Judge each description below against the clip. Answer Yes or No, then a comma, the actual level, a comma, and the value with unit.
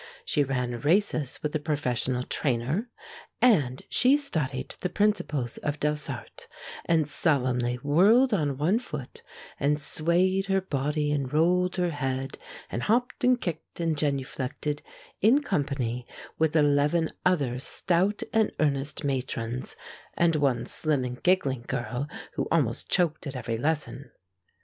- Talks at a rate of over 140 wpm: No, slow, 135 wpm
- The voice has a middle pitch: Yes, medium, 150 Hz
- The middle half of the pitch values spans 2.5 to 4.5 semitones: No, average, 5.0 semitones